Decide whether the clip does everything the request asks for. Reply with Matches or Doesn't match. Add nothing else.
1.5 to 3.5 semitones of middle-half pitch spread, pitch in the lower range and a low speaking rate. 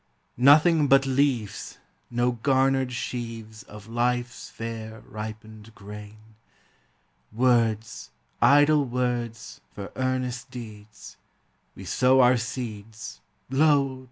Matches